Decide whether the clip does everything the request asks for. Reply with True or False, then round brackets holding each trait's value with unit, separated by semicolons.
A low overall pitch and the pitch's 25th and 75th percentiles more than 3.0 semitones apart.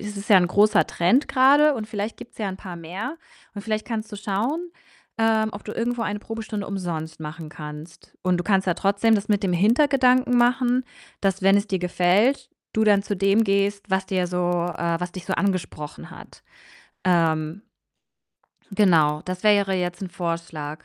False (200 Hz; 3.6 semitones)